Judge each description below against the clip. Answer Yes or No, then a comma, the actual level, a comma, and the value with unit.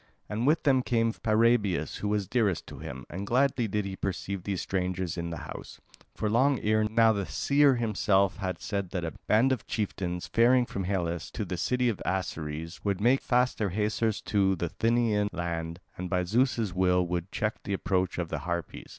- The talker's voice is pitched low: Yes, low, 100 Hz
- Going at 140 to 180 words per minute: No, average, 195 wpm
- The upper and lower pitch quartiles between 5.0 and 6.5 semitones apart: No, average, 4.1 semitones